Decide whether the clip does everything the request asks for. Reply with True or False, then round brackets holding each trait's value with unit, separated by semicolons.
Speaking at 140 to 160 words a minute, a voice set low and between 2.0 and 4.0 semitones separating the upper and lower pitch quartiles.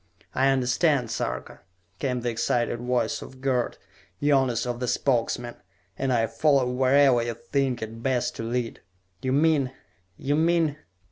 True (145 wpm; 125 Hz; 2.4 semitones)